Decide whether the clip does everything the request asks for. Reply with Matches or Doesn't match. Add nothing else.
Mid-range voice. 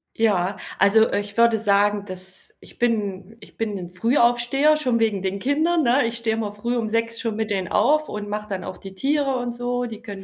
Doesn't match